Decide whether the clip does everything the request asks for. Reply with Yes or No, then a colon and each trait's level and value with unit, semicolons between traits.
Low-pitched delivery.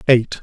Yes: low, 120 Hz